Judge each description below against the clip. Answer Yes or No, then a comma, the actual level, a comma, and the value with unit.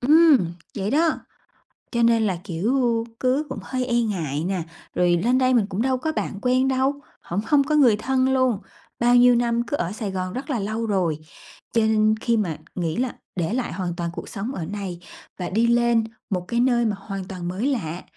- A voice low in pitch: No, high, 230 Hz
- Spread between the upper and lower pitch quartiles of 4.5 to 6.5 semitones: Yes, average, 5.1 semitones